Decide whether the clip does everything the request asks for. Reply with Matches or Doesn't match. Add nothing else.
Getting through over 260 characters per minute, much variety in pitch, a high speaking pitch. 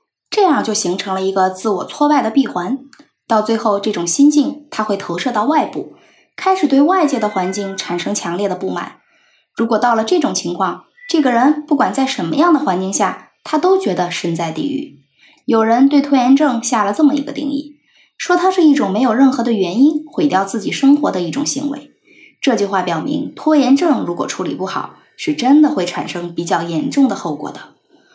Matches